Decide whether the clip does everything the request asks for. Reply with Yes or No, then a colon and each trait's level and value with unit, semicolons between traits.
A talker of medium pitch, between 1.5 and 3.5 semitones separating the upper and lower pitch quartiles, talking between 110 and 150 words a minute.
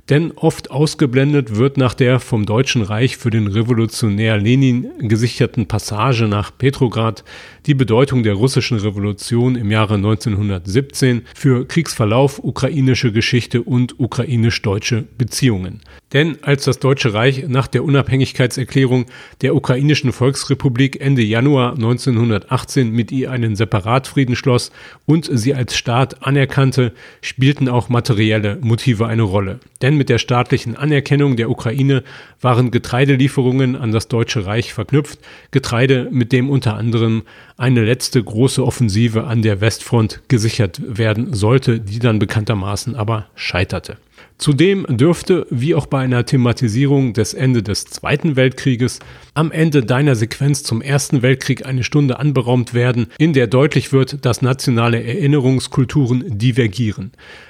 No: low, 125 Hz; average, 2.9 semitones; average, 135 wpm